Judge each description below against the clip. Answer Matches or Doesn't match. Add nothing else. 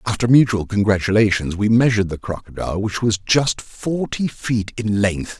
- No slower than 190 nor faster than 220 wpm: Doesn't match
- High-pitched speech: Doesn't match